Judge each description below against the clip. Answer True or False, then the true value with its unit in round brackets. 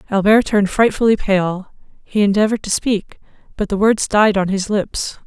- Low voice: False (205 Hz)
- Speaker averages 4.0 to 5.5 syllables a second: True (5.1 syllables/s)